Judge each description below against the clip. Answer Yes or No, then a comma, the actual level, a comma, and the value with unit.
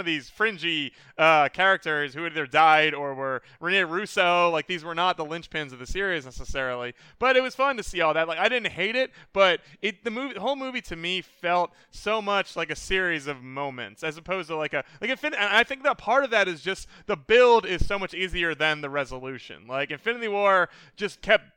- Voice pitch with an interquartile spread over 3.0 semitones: Yes, average, 4.9 semitones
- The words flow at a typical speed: No, fast, 230 wpm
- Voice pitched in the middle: Yes, medium, 175 Hz